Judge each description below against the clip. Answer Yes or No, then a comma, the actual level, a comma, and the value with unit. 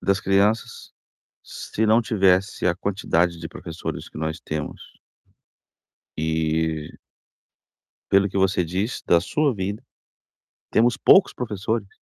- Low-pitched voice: Yes, very low, 95 Hz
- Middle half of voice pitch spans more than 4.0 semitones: Yes, average, 4.6 semitones